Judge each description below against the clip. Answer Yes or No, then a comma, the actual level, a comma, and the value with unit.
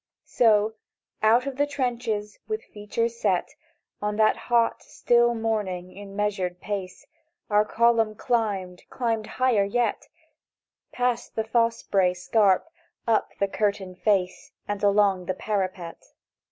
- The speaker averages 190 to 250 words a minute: No, average, 140 wpm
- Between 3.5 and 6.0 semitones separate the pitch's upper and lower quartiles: No, average, 2.9 semitones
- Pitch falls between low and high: No, high, 210 Hz